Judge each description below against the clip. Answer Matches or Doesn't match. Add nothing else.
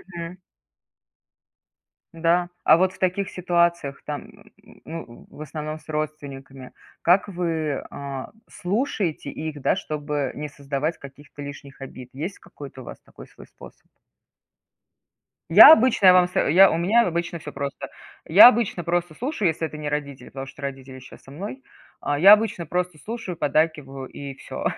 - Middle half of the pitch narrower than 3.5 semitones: Doesn't match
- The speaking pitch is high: Doesn't match